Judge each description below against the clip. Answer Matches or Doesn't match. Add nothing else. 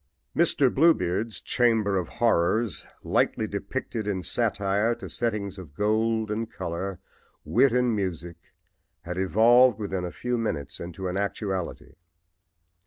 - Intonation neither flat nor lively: Matches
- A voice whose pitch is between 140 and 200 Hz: Doesn't match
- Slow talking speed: Matches